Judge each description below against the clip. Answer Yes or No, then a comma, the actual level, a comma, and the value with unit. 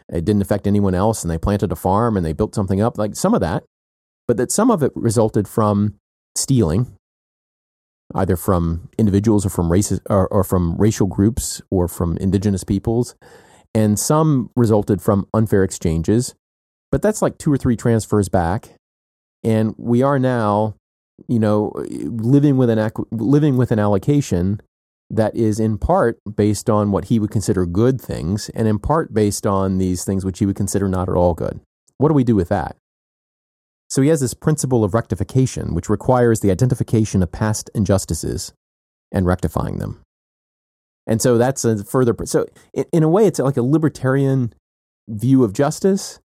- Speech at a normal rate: Yes, average, 175 wpm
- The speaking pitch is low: Yes, low, 105 Hz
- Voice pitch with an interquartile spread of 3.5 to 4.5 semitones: Yes, average, 4.1 semitones